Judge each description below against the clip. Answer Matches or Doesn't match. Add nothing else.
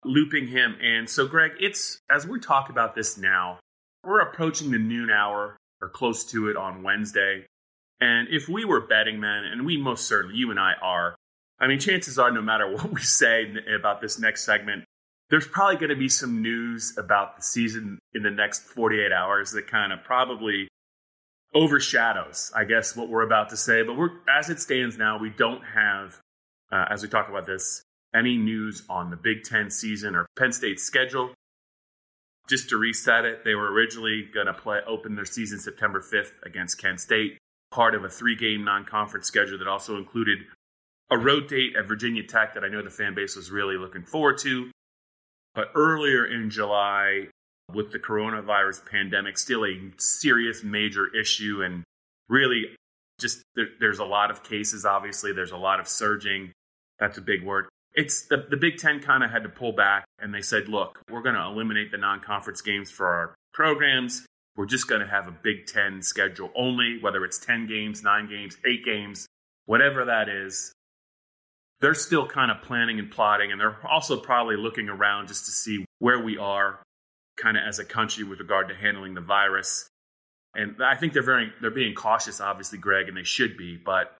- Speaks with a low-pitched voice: Matches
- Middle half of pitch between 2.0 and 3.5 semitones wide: Matches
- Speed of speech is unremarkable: Matches